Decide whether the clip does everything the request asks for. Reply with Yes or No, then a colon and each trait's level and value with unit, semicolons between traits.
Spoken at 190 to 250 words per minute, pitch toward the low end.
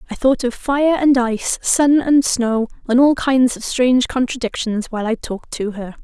No: average, 200 wpm; very high, 250 Hz